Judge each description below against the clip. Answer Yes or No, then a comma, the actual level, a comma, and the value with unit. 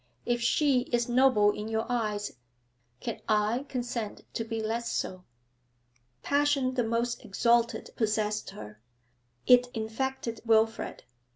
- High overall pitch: Yes, high, 230 Hz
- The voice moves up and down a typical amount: No, narrow, 2.3 semitones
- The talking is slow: Yes, slow, 120 wpm